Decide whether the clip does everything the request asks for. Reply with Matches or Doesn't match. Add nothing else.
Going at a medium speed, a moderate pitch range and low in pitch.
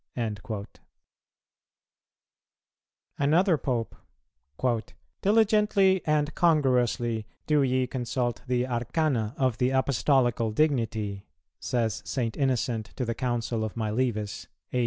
Doesn't match